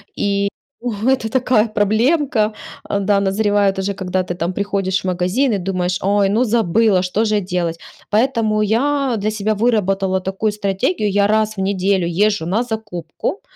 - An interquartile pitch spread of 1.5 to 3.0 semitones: Yes, narrow, 2.5 semitones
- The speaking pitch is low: No, high, 205 Hz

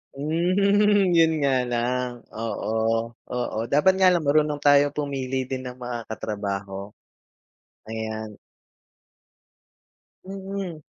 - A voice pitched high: No, medium, 140 Hz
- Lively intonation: Yes, wide, 6.3 semitones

